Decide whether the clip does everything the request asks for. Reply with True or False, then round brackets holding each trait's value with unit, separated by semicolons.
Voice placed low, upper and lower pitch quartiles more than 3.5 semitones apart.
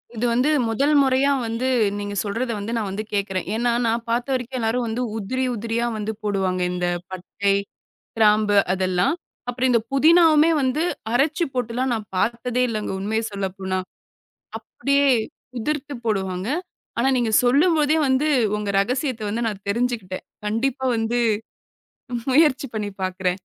False (230 Hz; 4.1 semitones)